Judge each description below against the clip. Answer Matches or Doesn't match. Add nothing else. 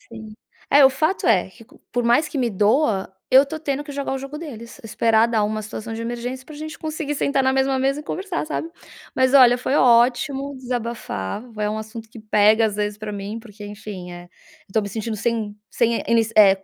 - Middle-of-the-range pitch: Doesn't match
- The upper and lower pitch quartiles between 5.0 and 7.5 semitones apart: Doesn't match